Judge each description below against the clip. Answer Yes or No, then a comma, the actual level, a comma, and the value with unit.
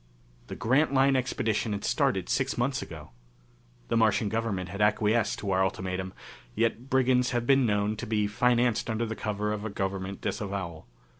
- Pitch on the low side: Yes, low, 110 Hz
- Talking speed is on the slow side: No, average, 160 wpm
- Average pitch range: Yes, average, 3.4 semitones